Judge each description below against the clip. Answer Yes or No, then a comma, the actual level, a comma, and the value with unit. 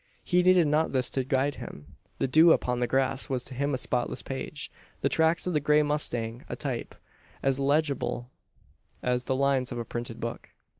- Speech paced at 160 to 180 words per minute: No, average, 195 wpm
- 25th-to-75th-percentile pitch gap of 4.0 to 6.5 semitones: No, average, 3.3 semitones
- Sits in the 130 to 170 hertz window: Yes, low, 135 Hz